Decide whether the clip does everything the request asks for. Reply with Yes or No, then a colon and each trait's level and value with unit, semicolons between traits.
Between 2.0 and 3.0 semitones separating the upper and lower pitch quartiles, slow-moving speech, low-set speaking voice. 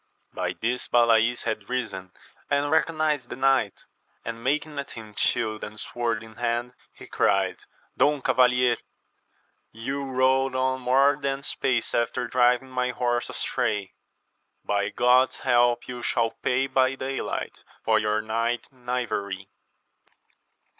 Yes: narrow, 2.5 semitones; slow, 130 wpm; low, 125 Hz